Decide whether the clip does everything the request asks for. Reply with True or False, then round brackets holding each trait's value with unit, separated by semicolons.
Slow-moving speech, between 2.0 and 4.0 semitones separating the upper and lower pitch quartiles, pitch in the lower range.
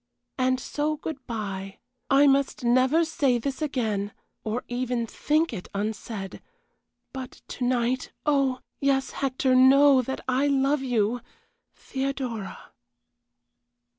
False (115 wpm; 2.8 semitones; 255 Hz)